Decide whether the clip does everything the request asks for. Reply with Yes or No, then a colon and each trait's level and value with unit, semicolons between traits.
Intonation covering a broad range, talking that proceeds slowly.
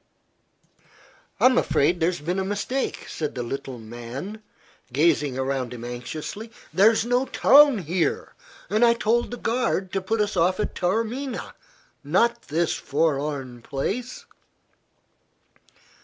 Yes: wide, 8.4 semitones; slow, 125 wpm